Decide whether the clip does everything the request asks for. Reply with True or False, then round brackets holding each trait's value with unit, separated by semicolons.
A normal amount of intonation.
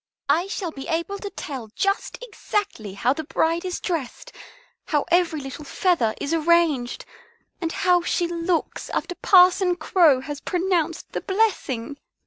True (4.0 semitones)